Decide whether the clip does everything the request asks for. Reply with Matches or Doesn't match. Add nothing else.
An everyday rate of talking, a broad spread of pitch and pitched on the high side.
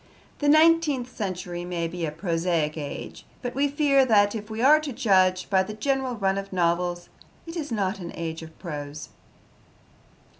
Matches